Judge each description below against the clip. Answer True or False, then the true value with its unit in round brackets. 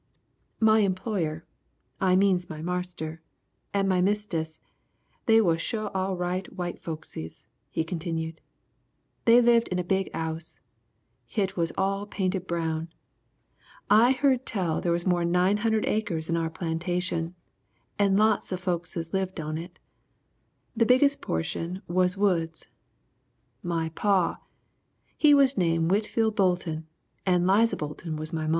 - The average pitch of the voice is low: False (180 Hz)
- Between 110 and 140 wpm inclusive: True (135 wpm)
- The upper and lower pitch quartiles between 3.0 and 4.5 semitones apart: True (3.5 semitones)